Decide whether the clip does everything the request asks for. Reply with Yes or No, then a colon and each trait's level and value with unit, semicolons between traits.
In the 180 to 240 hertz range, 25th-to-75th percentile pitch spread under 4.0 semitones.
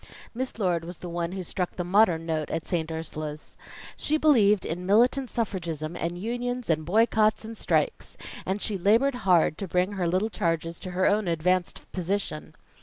No: medium, 185 Hz; average, 4.3 semitones